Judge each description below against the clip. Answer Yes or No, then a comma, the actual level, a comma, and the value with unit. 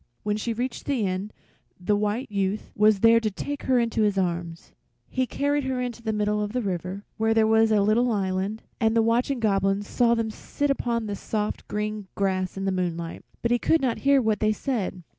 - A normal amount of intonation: Yes, average, 3.1 semitones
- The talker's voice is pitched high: Yes, high, 215 Hz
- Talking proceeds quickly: Yes, fast, 215 wpm